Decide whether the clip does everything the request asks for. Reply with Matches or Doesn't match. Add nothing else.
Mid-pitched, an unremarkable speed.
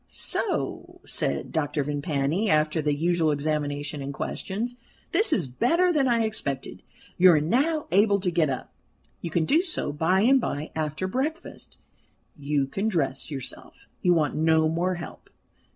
Matches